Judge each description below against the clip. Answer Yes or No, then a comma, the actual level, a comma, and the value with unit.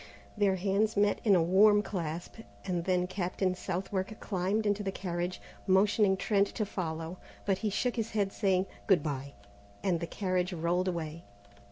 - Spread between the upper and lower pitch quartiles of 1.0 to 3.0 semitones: Yes, narrow, 2.6 semitones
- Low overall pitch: No, high, 190 Hz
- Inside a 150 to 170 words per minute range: Yes, average, 165 wpm